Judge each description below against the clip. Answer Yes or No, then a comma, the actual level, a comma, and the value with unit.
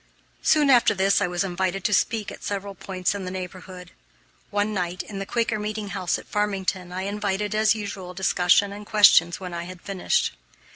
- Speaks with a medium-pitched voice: No, high, 195 Hz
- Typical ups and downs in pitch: No, narrow, 2.2 semitones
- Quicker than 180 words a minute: Yes, average, 190 wpm